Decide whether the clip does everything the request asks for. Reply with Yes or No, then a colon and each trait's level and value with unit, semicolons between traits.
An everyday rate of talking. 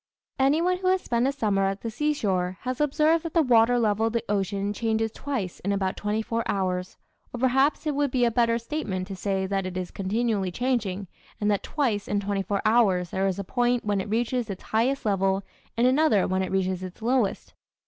No: fast, 215 wpm